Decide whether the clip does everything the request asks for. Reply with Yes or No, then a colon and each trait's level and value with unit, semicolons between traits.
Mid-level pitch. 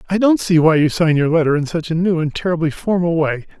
Yes: medium, 165 Hz